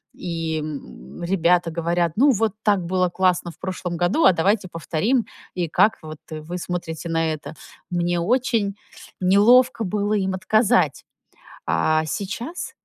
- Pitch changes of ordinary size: Yes, average, 3.7 semitones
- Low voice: No, medium, 180 Hz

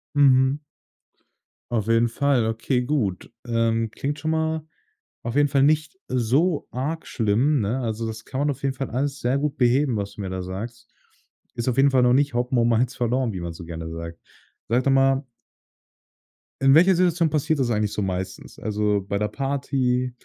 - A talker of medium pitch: No, low, 125 Hz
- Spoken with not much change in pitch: No, average, 4.1 semitones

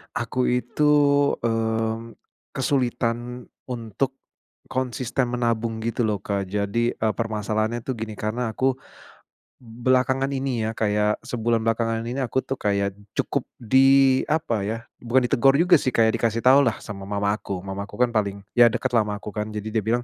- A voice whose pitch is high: No, low, 115 Hz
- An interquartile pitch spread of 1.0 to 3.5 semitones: Yes, average, 2.7 semitones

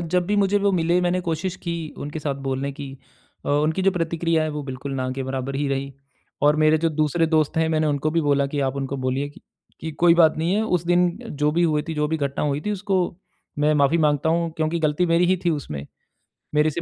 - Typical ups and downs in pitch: Yes, average, 3.1 semitones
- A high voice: No, medium, 155 Hz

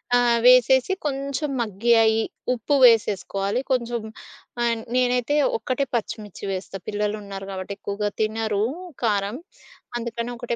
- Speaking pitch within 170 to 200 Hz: No, high, 230 Hz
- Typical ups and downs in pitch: Yes, average, 3.1 semitones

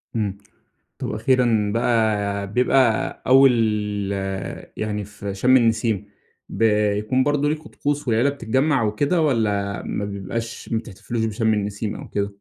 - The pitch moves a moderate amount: Yes, average, 3.7 semitones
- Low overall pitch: Yes, low, 110 Hz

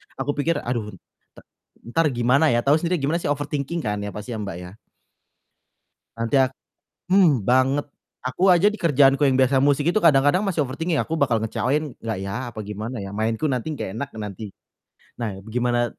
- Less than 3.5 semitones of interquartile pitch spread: No, average, 4.8 semitones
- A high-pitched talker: No, low, 130 Hz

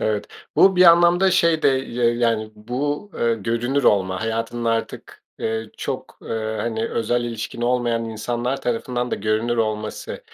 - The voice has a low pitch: Yes, low, 115 Hz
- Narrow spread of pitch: Yes, narrow, 2.0 semitones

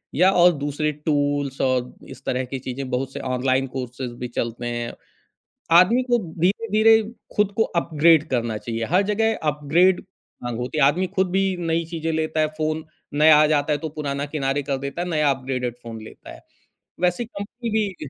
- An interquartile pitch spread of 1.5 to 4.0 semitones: No, average, 5.3 semitones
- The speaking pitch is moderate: Yes, medium, 150 Hz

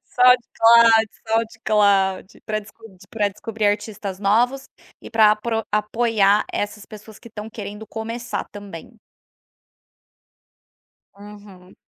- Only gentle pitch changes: Yes, narrow, 1.8 semitones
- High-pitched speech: Yes, high, 215 Hz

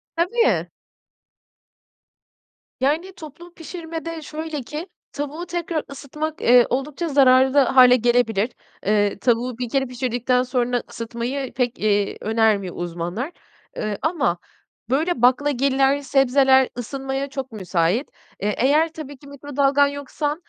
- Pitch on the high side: Yes, very high, 270 Hz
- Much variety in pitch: No, average, 3.6 semitones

